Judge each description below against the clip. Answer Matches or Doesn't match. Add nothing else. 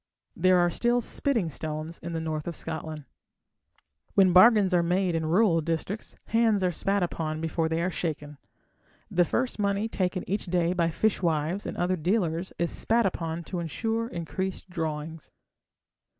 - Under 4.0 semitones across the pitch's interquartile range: Matches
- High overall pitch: Doesn't match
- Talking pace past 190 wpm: Doesn't match